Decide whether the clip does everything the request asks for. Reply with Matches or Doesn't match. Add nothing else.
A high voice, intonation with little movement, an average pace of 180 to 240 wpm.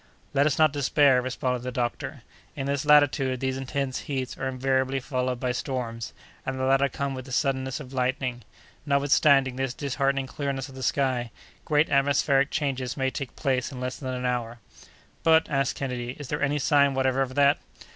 Doesn't match